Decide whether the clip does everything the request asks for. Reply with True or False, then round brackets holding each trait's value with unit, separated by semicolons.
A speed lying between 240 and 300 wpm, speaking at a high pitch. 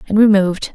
True (245 wpm; 200 Hz)